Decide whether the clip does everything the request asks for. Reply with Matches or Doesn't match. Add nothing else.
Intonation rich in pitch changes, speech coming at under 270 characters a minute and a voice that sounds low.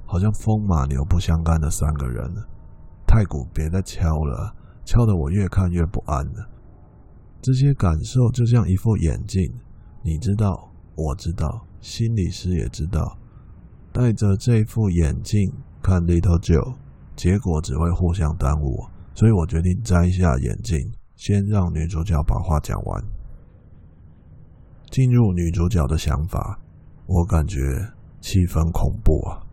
Doesn't match